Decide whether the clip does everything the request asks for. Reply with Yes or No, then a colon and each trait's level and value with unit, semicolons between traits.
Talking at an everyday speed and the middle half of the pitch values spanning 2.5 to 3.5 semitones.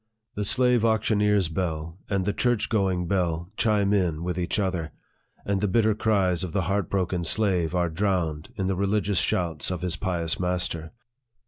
Yes: average, 175 wpm; average, 3.1 semitones